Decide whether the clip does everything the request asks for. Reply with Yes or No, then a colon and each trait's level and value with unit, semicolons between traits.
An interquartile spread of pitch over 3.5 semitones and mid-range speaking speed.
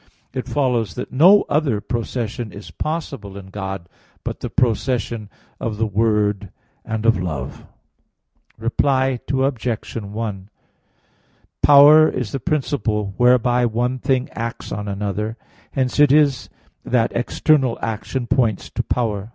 No: average, 3.9 semitones; slow, 125 wpm